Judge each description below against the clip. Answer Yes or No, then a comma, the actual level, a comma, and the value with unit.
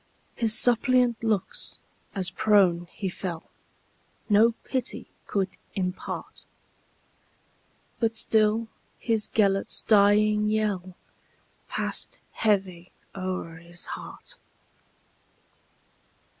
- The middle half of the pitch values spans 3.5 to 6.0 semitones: No, average, 3.0 semitones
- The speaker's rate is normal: No, slow, 70 wpm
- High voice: Yes, high, 210 Hz